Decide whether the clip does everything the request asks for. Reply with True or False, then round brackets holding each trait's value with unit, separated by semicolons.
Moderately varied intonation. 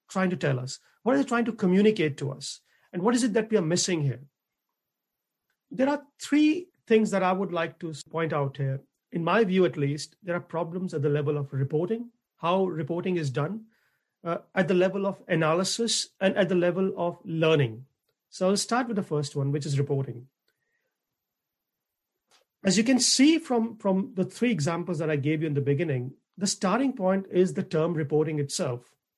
False (5.8 semitones)